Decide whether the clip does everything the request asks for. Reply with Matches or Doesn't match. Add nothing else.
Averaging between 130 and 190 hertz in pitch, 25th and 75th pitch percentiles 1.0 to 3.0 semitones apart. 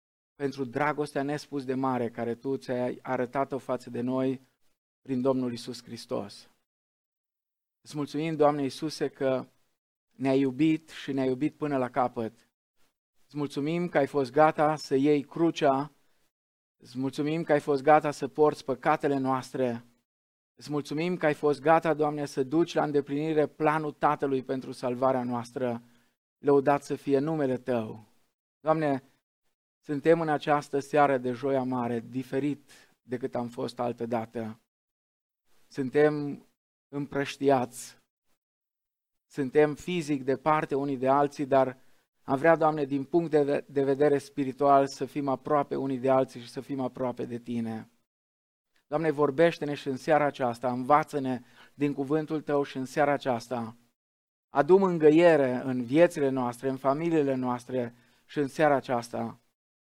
Matches